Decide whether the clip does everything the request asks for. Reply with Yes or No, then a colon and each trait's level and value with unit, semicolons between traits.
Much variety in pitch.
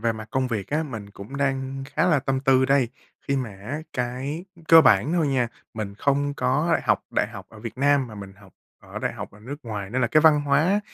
No: average, 4.6 semitones